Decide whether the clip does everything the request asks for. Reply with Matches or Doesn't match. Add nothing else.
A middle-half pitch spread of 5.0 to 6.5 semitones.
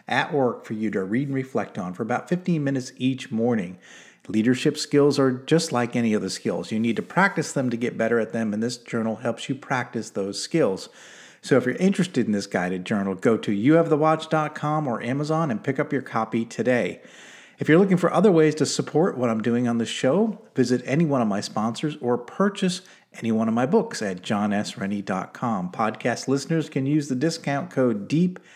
Matches